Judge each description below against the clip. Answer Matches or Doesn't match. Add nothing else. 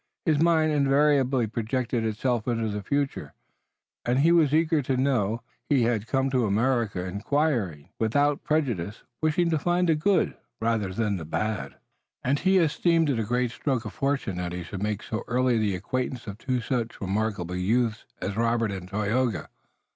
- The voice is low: Matches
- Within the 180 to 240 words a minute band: Doesn't match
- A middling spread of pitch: Matches